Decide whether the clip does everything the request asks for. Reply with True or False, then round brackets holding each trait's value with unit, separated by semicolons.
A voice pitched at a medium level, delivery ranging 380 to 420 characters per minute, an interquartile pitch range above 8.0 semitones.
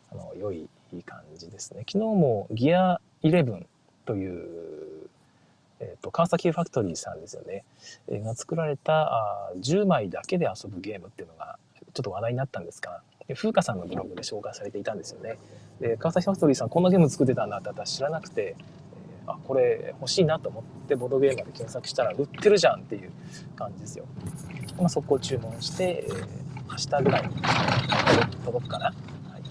False (165 Hz; 385 characters per minute; 6.9 semitones)